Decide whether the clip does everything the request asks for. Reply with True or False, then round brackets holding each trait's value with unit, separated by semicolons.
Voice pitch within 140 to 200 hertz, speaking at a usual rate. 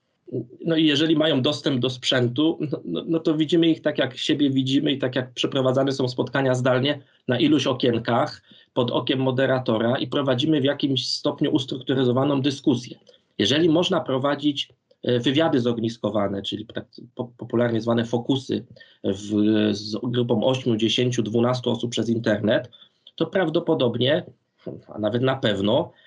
False (130 Hz; 140 wpm)